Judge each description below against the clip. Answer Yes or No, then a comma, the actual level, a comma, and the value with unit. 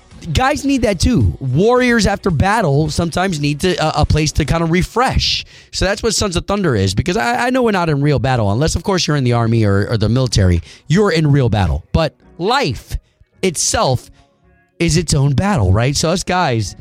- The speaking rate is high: Yes, fast, 210 wpm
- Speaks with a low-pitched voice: No, medium, 150 Hz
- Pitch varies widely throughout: Yes, wide, 7.9 semitones